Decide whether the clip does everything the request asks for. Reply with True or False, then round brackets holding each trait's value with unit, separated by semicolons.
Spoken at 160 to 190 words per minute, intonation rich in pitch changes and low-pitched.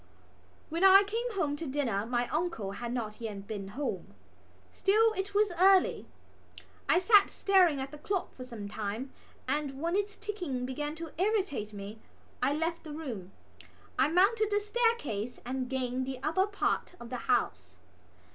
False (165 wpm; 8.1 semitones; 295 Hz)